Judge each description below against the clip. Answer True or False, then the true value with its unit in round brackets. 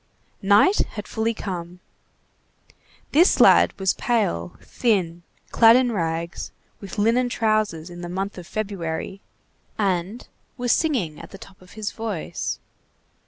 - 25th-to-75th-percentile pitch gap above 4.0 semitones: True (4.4 semitones)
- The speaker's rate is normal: False (130 wpm)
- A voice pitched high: True (200 Hz)